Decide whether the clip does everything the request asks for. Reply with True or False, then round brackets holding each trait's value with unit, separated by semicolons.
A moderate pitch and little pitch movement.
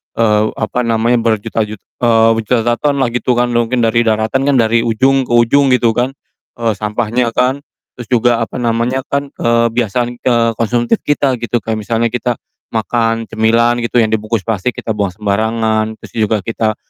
False (115 Hz; 1.7 semitones)